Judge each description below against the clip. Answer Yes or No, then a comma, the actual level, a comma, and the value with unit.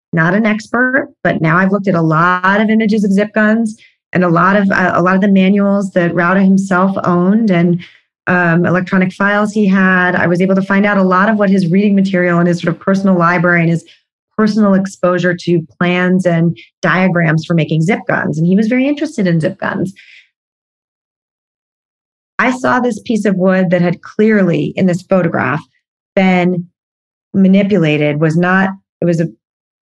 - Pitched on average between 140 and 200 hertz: Yes, medium, 185 Hz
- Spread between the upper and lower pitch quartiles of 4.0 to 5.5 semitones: No, narrow, 2.6 semitones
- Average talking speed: Yes, average, 185 wpm